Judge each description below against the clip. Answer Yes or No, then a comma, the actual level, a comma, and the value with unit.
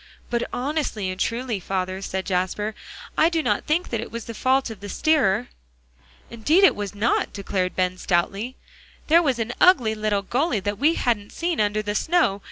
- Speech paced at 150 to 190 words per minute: Yes, average, 185 wpm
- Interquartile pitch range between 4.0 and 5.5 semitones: Yes, average, 5.1 semitones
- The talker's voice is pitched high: Yes, high, 220 Hz